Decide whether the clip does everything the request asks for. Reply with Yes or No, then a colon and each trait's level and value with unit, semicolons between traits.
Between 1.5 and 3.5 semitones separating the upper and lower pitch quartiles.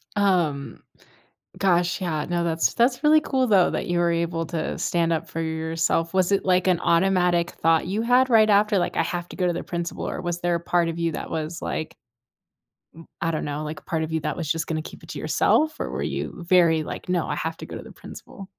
Yes: narrow, 2.5 semitones